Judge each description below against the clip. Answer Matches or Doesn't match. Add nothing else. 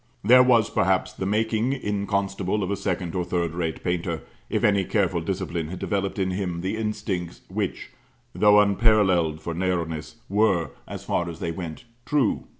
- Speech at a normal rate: Matches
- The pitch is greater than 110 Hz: Doesn't match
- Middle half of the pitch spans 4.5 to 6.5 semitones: Doesn't match